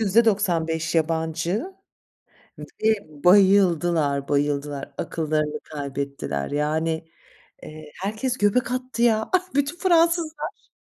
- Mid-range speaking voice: Yes, medium, 170 Hz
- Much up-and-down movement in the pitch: Yes, wide, 7.4 semitones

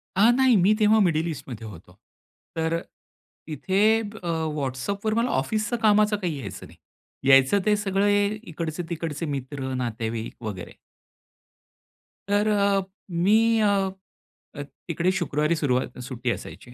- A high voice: No, medium, 170 Hz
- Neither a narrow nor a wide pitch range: No, wide, 7.5 semitones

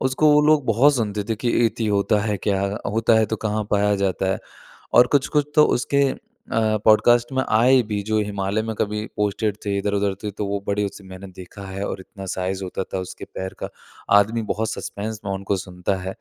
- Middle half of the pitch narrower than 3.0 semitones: Yes, narrow, 2.4 semitones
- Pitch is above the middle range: No, low, 105 Hz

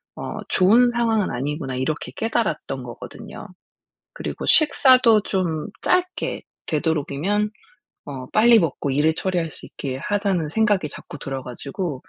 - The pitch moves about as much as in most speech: No, wide, 7.4 semitones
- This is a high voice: No, medium, 170 Hz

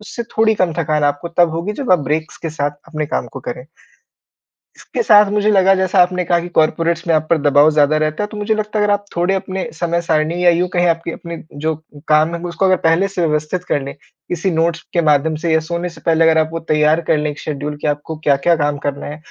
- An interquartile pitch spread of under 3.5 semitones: Yes, average, 2.9 semitones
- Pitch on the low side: No, medium, 165 Hz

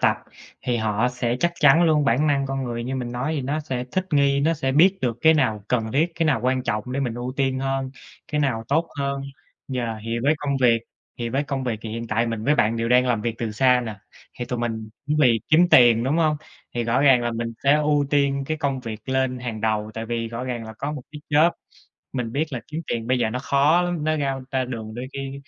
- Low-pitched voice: Yes, low, 130 Hz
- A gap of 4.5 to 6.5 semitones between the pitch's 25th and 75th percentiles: No, average, 3.5 semitones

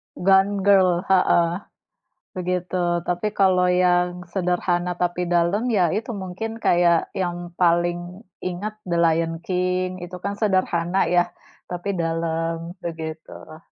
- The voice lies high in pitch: No, medium, 180 Hz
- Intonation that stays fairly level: Yes, narrow, 1.5 semitones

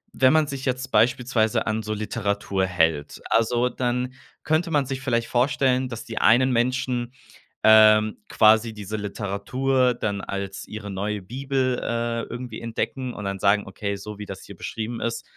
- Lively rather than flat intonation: No, average, 3.5 semitones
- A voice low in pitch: Yes, low, 115 Hz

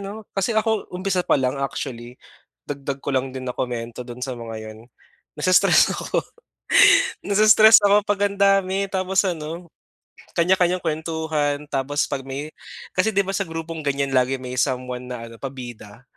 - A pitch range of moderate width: No, wide, 6.9 semitones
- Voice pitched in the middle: Yes, medium, 150 Hz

